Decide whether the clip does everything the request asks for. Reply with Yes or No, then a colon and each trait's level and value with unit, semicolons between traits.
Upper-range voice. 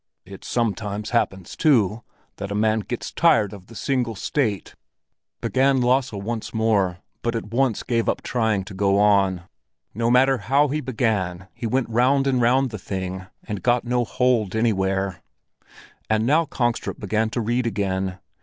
No: low, 110 Hz